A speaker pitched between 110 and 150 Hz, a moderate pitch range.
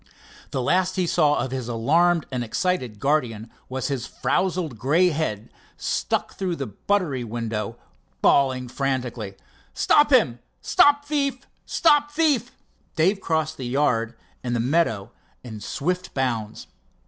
No: medium, 140 Hz; wide, 7.2 semitones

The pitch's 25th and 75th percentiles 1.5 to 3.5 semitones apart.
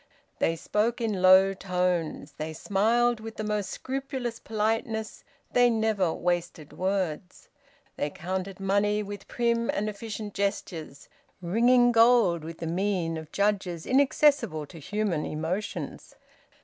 No: average, 4.3 semitones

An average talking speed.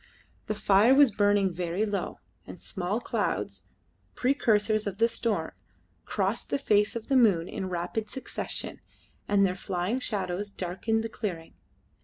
Yes: average, 145 wpm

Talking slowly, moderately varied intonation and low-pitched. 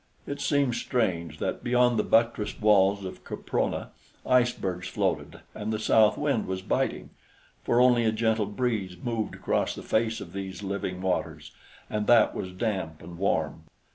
No: average, 160 wpm; average, 4.0 semitones; low, 105 Hz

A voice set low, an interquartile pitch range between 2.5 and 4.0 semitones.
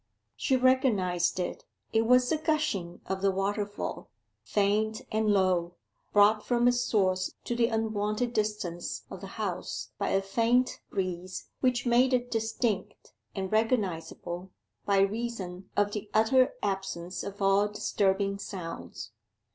No: high, 205 Hz; average, 3.5 semitones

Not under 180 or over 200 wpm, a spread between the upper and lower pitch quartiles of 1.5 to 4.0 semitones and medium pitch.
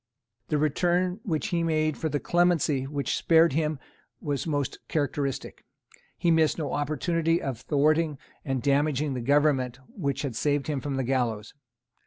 No: average, 155 wpm; average, 2.9 semitones; medium, 150 Hz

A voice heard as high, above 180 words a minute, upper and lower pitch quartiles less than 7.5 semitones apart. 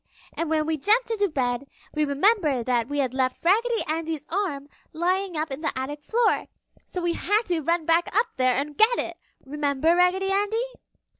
Yes: very high, 320 Hz; average, 190 wpm; wide, 5.5 semitones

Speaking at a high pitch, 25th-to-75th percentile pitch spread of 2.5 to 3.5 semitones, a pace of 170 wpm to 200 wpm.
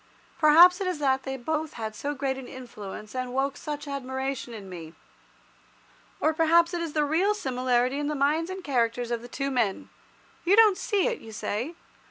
No: very high, 275 Hz; average, 4.5 semitones; average, 195 wpm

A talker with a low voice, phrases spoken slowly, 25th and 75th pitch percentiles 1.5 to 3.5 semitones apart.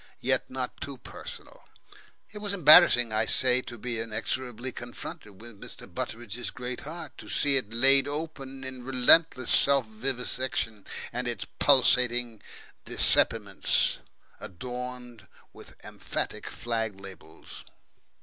Yes: low, 125 Hz; slow, 120 wpm; average, 2.8 semitones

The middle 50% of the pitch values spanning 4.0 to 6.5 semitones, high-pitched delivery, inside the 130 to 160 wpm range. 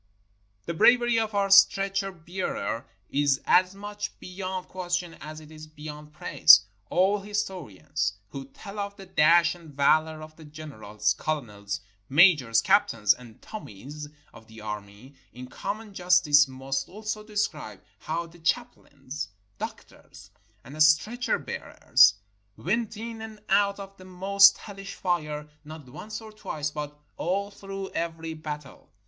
No: average, 5.2 semitones; medium, 165 Hz; average, 140 wpm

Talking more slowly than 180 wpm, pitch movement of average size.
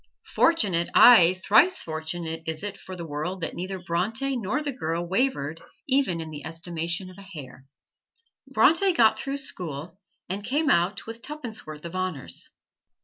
No: average, 160 wpm; wide, 6.1 semitones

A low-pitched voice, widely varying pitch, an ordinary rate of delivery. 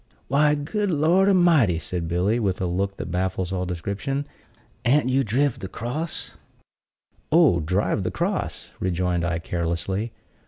Yes: low, 100 Hz; wide, 8.3 semitones; average, 145 wpm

